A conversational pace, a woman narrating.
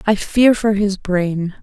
Yes: average, 185 wpm; female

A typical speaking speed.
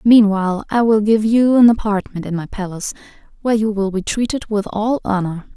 Yes: average, 195 wpm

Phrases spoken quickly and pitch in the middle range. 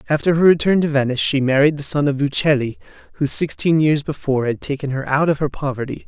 Yes: fast, 225 wpm; medium, 145 Hz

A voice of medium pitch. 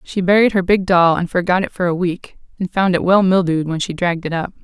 Yes: medium, 180 Hz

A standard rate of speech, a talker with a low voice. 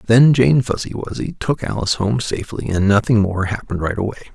Yes: average, 195 wpm; low, 110 Hz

